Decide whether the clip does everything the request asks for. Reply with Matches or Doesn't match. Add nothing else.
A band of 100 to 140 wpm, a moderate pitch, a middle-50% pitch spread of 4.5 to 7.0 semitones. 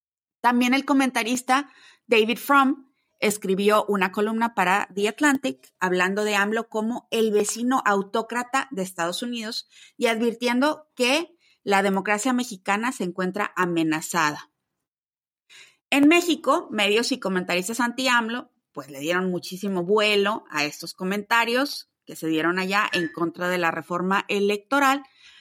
Doesn't match